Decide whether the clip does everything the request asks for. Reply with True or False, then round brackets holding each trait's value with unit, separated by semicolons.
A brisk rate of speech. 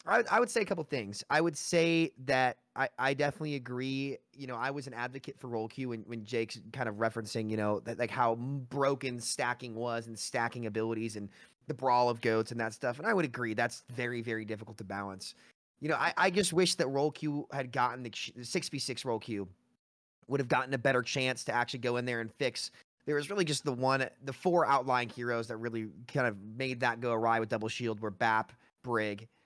True (225 wpm)